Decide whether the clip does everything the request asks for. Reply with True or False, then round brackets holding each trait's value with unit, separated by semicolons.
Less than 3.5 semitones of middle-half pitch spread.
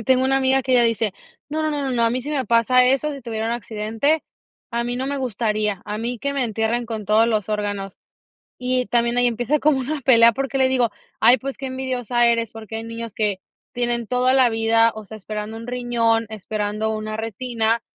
True (2.7 semitones)